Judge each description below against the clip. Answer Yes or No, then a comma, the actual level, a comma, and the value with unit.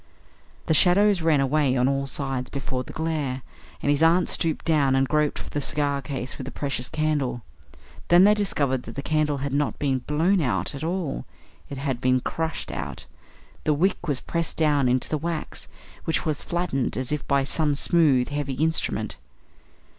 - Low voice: No, medium, 145 Hz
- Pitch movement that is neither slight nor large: Yes, average, 3.1 semitones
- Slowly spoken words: No, average, 185 wpm